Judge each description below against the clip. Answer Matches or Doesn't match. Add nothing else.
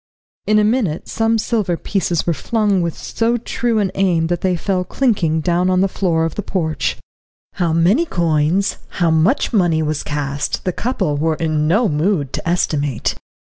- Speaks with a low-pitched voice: Doesn't match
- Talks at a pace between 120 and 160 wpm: Doesn't match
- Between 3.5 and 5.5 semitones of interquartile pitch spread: Matches